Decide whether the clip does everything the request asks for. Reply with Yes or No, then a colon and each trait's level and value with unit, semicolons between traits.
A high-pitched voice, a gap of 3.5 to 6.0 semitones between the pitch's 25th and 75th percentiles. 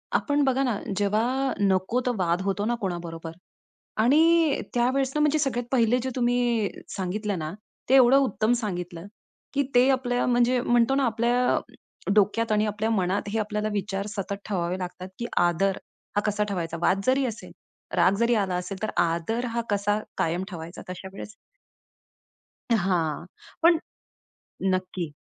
Yes: high, 210 Hz; average, 4.7 semitones